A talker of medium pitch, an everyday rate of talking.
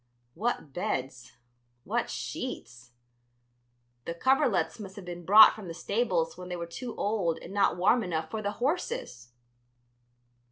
Yes: medium, 180 Hz; average, 145 wpm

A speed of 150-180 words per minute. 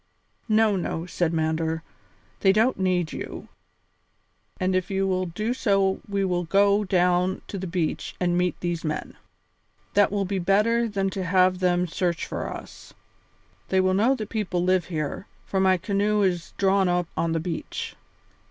Yes: average, 170 wpm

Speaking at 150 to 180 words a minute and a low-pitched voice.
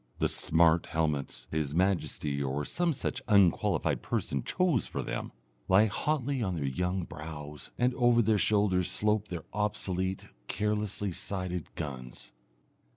No: slow, 135 wpm; very low, 95 Hz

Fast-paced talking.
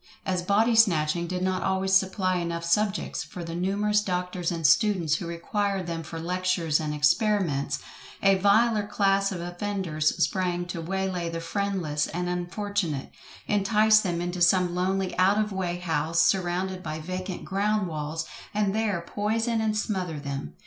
No: average, 160 wpm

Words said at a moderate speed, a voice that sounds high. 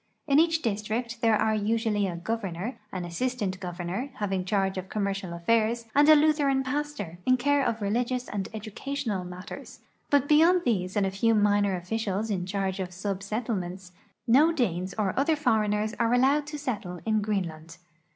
Yes: average, 175 wpm; high, 215 Hz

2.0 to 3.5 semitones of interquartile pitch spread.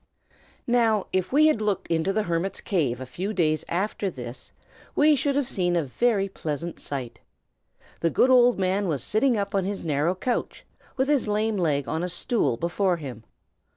No: average, 5.3 semitones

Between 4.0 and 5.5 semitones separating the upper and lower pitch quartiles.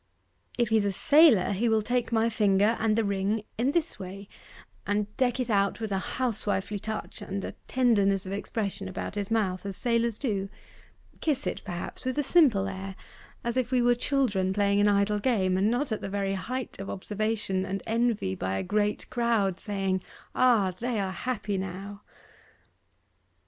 No: average, 3.3 semitones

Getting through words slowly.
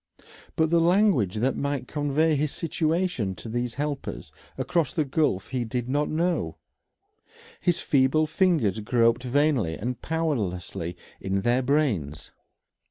Yes: slow, 130 wpm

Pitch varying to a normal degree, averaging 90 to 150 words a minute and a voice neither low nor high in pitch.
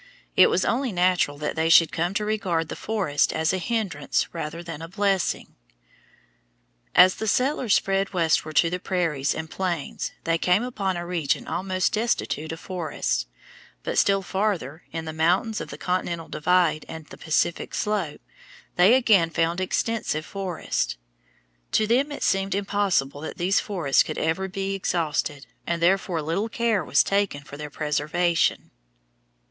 No: average, 3.6 semitones; average, 160 wpm; medium, 180 Hz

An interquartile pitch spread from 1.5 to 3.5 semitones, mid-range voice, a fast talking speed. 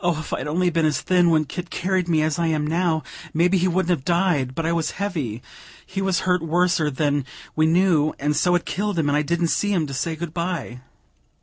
Yes: average, 2.8 semitones; medium, 165 Hz; fast, 230 wpm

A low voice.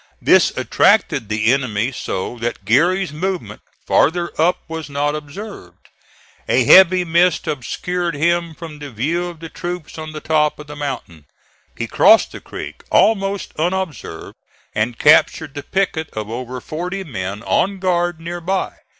No: medium, 160 Hz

